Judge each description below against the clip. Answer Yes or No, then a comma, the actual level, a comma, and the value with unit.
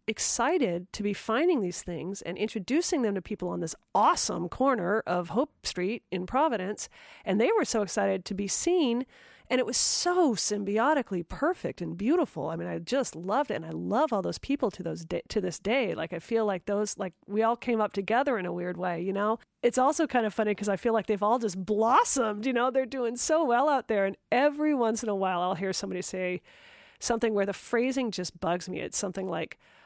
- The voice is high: Yes, high, 215 Hz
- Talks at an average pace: No, fast, 225 wpm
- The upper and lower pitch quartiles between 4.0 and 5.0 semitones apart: No, wide, 5.4 semitones